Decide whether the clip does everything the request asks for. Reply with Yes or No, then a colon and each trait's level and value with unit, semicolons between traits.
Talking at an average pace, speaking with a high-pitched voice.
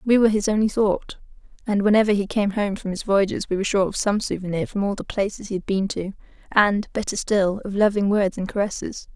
No: fast, 230 wpm; high, 200 Hz